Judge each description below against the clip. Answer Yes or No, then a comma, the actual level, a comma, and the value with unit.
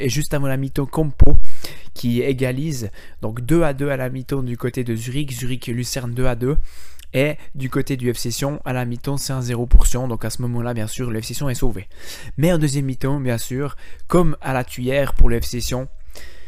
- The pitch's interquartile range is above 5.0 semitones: No, narrow, 2.5 semitones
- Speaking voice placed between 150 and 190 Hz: No, low, 130 Hz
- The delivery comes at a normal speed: Yes, average, 210 wpm